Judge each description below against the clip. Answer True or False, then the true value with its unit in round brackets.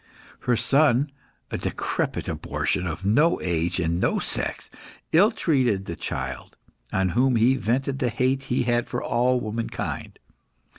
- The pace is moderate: True (145 wpm)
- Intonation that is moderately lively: False (5.7 semitones)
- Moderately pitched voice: False (120 Hz)